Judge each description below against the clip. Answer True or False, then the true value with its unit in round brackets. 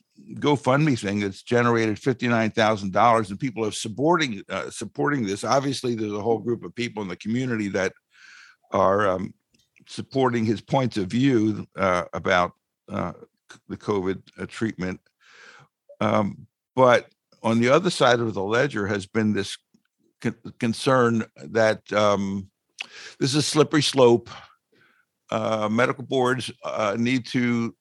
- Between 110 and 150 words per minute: True (140 wpm)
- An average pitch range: True (3.4 semitones)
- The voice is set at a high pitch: False (115 Hz)